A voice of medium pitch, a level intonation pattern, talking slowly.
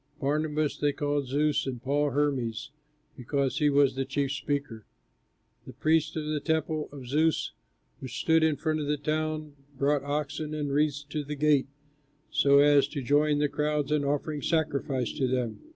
No: medium, 145 Hz; narrow, 1.6 semitones; average, 170 wpm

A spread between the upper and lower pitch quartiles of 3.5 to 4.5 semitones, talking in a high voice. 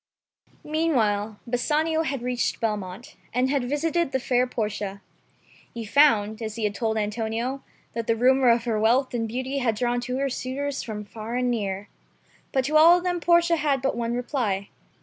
Yes: average, 3.9 semitones; high, 245 Hz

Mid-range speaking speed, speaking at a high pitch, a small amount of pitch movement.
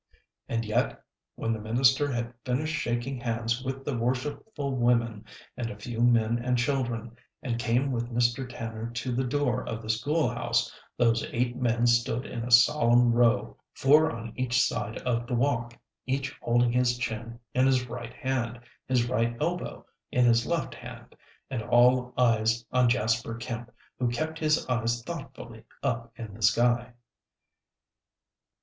No: average, 160 wpm; low, 120 Hz; narrow, 1.6 semitones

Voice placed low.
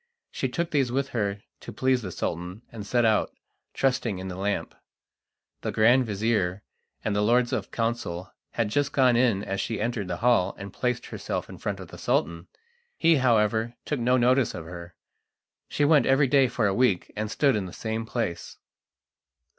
Yes: low, 115 Hz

